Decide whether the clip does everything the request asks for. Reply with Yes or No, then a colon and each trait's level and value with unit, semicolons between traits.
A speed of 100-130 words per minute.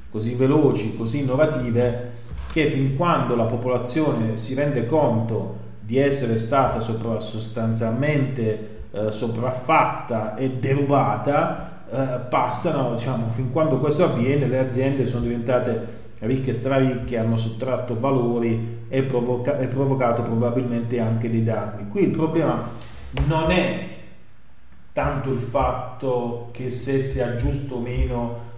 Yes: average, 125 wpm